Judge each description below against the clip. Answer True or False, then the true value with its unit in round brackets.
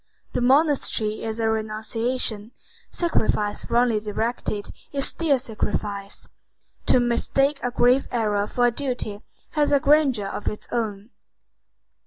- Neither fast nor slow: False (125 wpm)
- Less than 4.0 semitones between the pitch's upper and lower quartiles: True (3.6 semitones)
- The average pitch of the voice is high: True (235 Hz)